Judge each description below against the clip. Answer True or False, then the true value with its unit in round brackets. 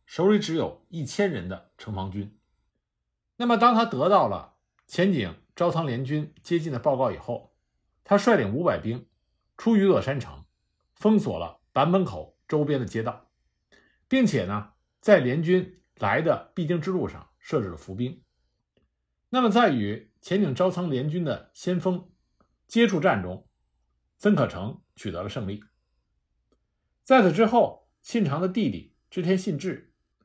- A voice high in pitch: False (165 Hz)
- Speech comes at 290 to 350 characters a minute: False (215 characters per minute)